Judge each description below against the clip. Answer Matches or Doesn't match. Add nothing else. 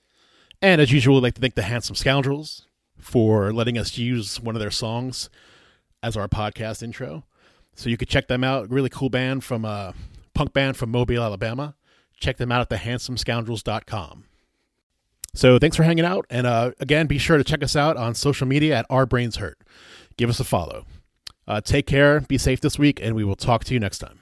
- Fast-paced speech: Matches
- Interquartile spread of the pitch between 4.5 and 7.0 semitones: Doesn't match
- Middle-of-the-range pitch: Doesn't match